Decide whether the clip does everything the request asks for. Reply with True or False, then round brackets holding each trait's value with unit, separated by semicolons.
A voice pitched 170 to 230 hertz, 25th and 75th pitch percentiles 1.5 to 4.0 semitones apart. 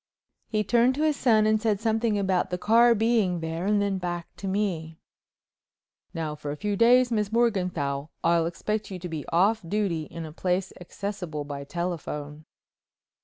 False (190 Hz; 4.7 semitones)